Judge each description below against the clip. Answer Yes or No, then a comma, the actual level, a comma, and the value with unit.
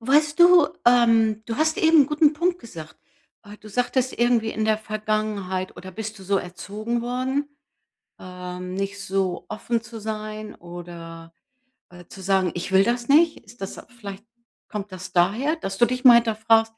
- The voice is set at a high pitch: Yes, high, 215 Hz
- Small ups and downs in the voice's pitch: No, average, 4.4 semitones